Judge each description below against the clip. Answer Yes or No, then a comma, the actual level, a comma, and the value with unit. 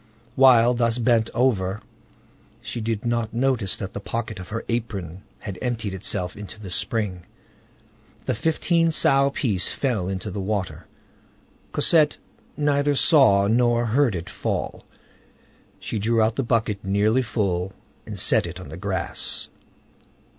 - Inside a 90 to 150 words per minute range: Yes, average, 140 wpm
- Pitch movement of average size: Yes, average, 4.0 semitones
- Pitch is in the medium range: No, low, 110 Hz